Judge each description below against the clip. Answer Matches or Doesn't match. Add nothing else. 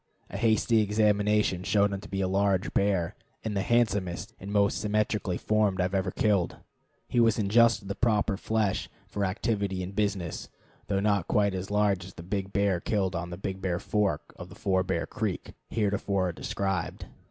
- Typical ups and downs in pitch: Doesn't match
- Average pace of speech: Matches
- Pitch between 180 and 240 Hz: Doesn't match